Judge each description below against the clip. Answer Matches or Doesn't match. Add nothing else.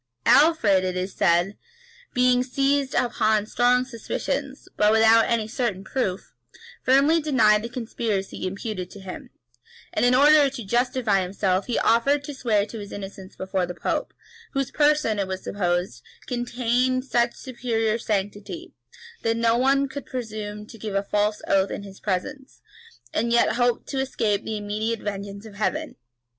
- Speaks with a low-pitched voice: Doesn't match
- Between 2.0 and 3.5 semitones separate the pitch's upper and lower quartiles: Doesn't match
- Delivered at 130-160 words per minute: Matches